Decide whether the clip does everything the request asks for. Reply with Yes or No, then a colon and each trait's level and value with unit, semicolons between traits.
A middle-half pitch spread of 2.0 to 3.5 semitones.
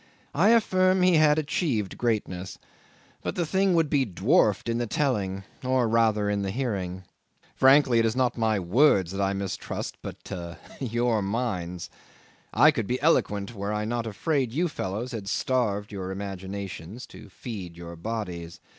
No: average, 5.1 semitones